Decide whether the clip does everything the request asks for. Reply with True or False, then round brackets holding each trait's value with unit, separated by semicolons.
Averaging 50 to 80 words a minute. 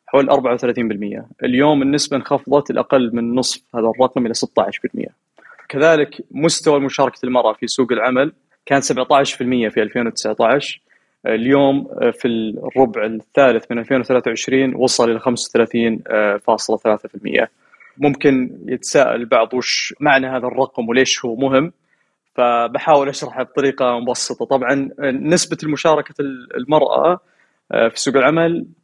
False (110 wpm)